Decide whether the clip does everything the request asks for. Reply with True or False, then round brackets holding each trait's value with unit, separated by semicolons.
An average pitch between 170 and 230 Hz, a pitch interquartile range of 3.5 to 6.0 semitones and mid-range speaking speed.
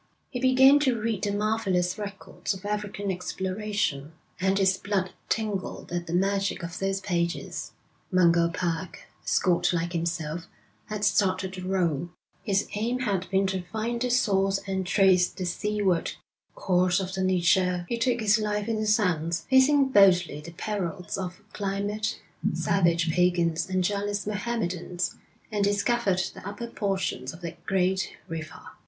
False (190 Hz; 2.8 semitones; 150 wpm)